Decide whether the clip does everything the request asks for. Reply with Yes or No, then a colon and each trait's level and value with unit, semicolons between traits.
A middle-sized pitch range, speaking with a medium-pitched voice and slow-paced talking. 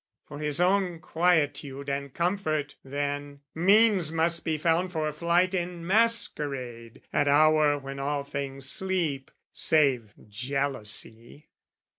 Yes: average, 3.7 semitones; medium, 150 Hz; slow, 115 wpm